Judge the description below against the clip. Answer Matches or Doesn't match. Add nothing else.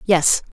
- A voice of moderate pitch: Matches